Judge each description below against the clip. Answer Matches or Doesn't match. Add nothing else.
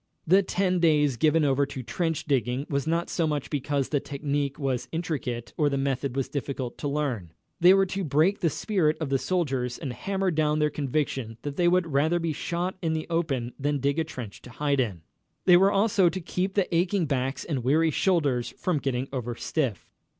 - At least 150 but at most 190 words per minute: Doesn't match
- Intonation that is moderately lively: Matches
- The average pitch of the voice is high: Doesn't match